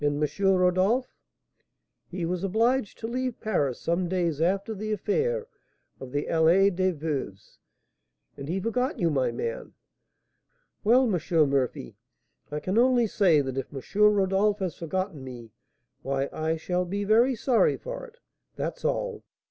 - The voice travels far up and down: Yes, wide, 6.5 semitones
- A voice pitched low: No, medium, 185 Hz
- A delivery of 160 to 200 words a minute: No, average, 145 wpm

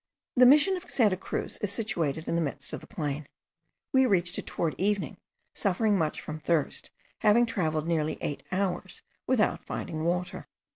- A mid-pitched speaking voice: Yes, medium, 180 Hz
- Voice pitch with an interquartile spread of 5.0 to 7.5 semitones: Yes, average, 5.3 semitones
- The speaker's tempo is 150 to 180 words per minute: Yes, average, 175 wpm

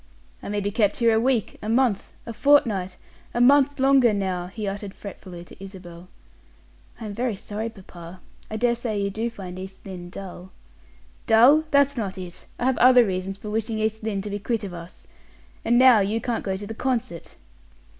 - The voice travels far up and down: No, average, 3.8 semitones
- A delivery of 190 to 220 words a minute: Yes, average, 195 wpm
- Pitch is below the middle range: No, high, 210 Hz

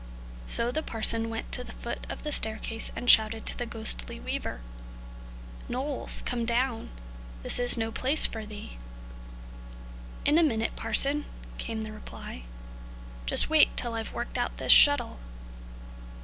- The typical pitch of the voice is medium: No, high, 230 Hz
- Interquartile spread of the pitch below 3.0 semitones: Yes, narrow, 2.6 semitones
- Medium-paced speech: Yes, average, 150 wpm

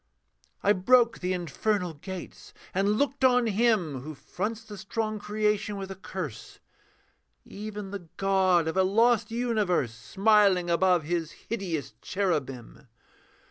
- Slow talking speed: Yes, slow, 130 wpm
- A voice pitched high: Yes, high, 195 Hz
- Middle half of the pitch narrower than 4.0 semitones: Yes, average, 3.6 semitones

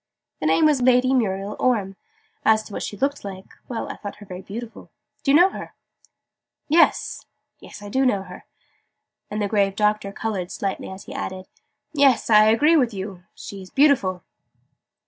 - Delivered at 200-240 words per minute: No, average, 175 wpm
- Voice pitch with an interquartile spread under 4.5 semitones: No, average, 4.8 semitones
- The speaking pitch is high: Yes, high, 210 Hz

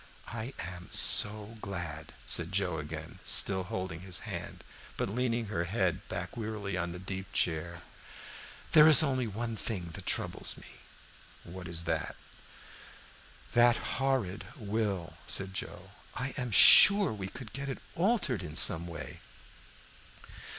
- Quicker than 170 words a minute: No, average, 140 wpm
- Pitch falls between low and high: No, very low, 95 Hz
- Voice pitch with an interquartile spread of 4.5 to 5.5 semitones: Yes, average, 5.1 semitones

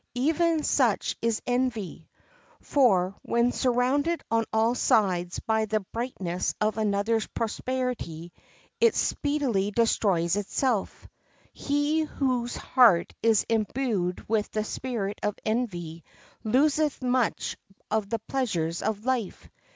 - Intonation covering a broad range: No, average, 4.2 semitones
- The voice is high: Yes, high, 225 Hz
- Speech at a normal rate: No, slow, 110 wpm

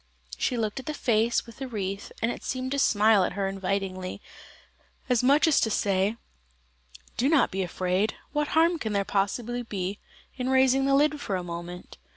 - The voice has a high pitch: Yes, high, 220 Hz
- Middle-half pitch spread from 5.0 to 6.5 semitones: Yes, wide, 5.4 semitones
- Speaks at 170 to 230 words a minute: Yes, average, 190 wpm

